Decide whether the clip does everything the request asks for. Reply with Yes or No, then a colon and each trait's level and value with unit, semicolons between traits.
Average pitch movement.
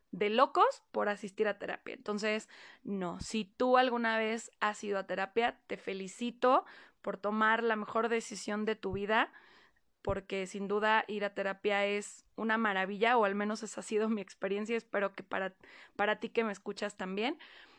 No: narrow, 2.3 semitones